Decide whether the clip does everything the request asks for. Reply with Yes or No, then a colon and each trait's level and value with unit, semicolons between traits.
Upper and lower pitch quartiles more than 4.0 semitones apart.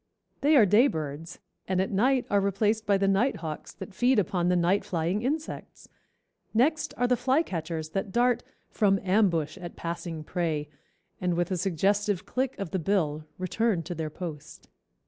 Yes: average, 4.6 semitones